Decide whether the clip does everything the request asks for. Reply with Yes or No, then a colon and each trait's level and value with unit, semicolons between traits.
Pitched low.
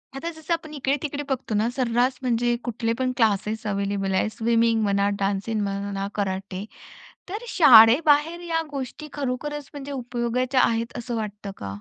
No: high, 240 Hz